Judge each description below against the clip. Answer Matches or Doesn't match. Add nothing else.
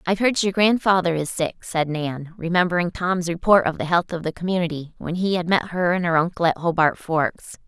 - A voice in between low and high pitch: Matches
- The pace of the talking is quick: Matches